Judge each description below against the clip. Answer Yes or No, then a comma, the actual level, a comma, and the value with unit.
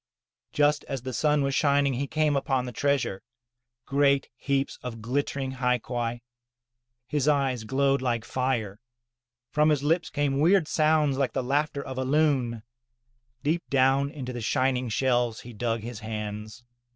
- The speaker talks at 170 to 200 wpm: No, average, 155 wpm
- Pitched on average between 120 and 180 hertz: Yes, low, 135 Hz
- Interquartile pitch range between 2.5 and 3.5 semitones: Yes, average, 2.8 semitones